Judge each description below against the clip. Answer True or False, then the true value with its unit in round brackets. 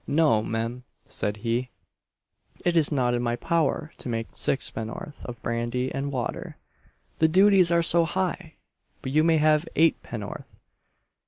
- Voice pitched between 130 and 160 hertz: True (140 Hz)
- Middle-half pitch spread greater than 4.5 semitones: True (5.6 semitones)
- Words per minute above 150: False (145 wpm)